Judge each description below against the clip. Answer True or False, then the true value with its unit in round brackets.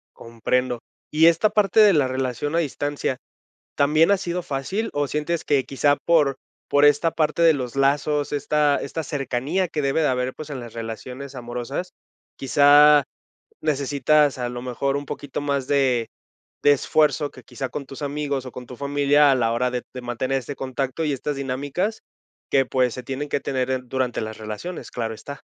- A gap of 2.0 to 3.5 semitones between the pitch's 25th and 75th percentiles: True (2.6 semitones)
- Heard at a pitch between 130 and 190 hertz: True (140 Hz)